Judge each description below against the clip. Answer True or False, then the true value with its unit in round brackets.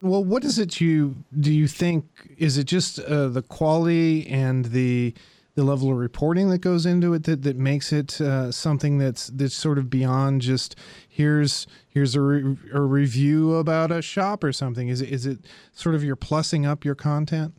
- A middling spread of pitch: True (3.0 semitones)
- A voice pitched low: False (145 Hz)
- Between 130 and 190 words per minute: False (200 wpm)